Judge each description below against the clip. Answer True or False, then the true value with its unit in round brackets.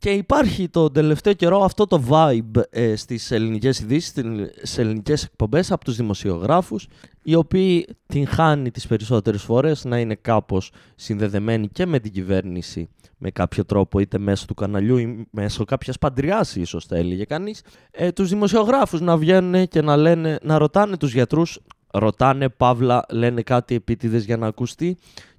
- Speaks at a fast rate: False (160 wpm)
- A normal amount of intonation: False (7.1 semitones)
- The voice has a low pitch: True (125 Hz)